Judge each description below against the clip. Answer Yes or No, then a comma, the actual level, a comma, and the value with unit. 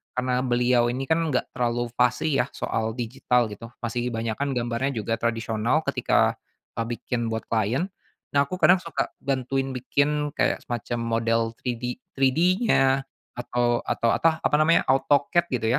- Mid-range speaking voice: No, low, 125 Hz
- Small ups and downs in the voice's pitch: No, average, 3.0 semitones